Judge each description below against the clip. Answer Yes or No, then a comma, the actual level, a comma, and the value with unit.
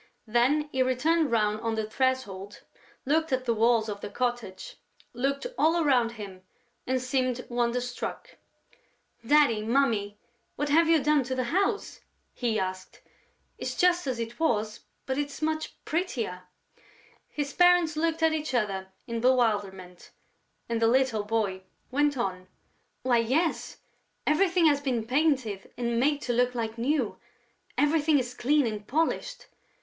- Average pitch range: Yes, average, 4.8 semitones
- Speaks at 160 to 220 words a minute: No, average, 145 wpm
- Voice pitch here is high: Yes, very high, 250 Hz